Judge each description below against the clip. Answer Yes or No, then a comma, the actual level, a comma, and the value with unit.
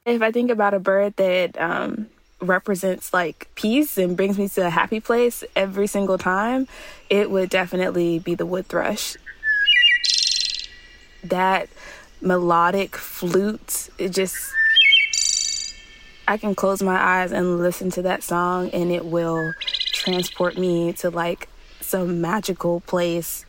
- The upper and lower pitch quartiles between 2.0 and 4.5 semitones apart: Yes, average, 3.7 semitones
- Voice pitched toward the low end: No, high, 190 Hz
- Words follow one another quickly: No, slow, 135 wpm